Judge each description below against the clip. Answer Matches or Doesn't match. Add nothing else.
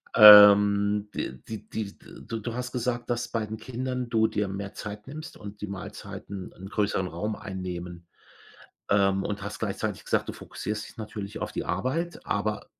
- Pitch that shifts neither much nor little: Doesn't match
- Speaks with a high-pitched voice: Doesn't match